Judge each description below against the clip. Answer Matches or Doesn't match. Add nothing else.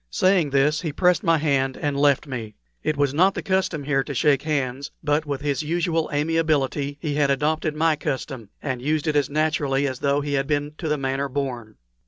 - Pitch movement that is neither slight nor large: Doesn't match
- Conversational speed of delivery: Doesn't match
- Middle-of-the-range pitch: Matches